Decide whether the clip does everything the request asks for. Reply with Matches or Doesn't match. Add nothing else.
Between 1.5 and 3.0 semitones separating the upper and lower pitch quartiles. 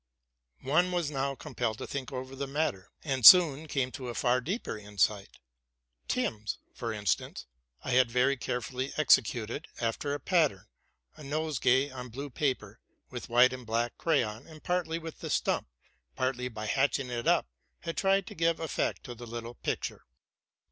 Doesn't match